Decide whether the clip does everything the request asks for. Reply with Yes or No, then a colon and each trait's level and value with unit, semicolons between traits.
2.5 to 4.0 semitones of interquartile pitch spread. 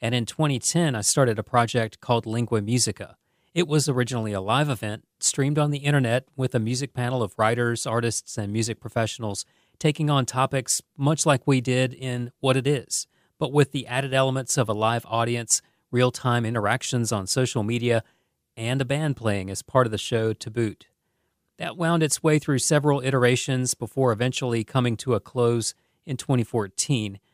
Yes: average, 3.1 semitones